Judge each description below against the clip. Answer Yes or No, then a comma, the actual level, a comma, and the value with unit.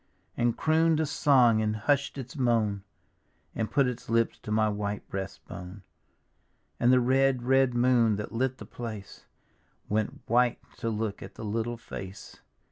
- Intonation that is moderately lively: Yes, average, 3.2 semitones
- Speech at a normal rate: Yes, average, 160 wpm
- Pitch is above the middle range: No, low, 115 Hz